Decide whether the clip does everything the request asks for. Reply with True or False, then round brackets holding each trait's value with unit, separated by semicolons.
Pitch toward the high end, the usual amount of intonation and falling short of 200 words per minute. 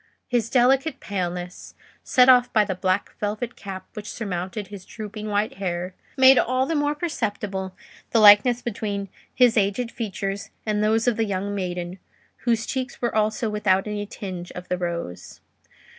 True (210 Hz; 3.9 semitones; 160 wpm)